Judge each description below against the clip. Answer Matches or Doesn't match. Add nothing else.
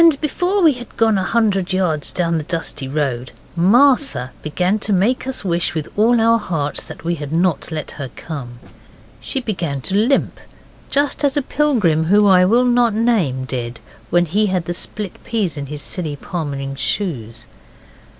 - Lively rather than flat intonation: Matches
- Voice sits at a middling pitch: Matches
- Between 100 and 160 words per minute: Doesn't match